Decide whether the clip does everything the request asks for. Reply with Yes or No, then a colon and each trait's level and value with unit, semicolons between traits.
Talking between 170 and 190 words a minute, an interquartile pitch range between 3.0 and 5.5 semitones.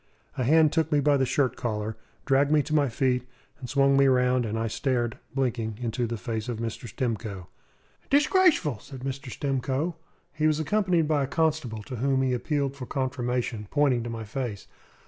Yes: average, 185 wpm; average, 3.6 semitones